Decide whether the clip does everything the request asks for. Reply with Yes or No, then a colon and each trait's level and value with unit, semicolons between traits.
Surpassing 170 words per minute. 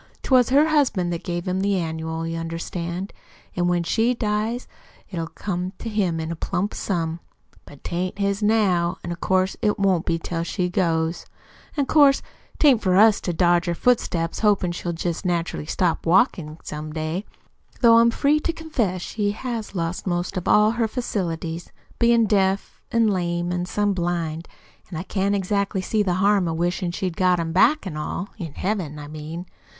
Yes: average, 180 wpm